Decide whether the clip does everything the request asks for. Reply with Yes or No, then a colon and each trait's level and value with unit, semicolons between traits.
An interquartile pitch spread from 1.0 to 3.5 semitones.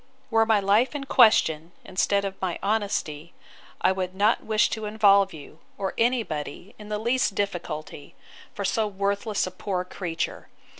Yes: average, 2.9 semitones